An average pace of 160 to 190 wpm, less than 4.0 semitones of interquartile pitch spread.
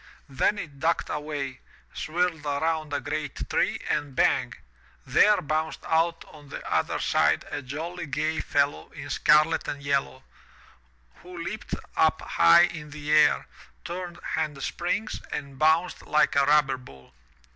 No: average, 145 wpm; narrow, 2.5 semitones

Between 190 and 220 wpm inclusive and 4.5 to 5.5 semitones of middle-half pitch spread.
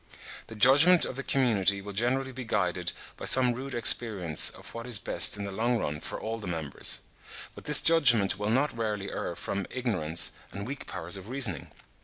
Yes: average, 195 wpm; average, 4.8 semitones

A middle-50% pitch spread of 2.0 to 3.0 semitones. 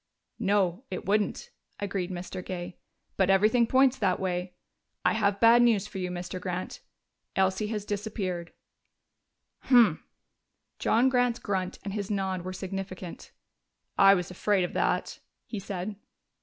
Yes: narrow, 2.5 semitones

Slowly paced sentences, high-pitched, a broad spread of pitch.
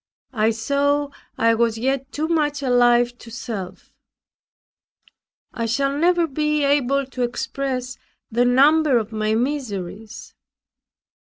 No: slow, 115 wpm; very high, 255 Hz; average, 3.7 semitones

